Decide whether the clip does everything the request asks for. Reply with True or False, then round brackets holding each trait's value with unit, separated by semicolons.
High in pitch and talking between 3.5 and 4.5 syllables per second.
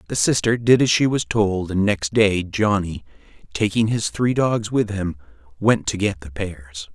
False (100 Hz; 4.3 syllables/s)